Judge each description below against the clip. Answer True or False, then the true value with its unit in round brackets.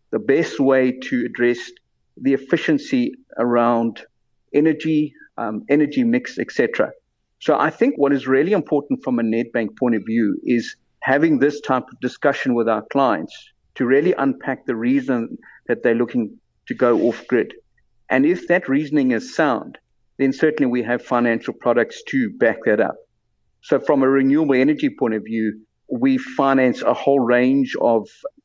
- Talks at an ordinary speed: True (165 wpm)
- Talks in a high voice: False (140 Hz)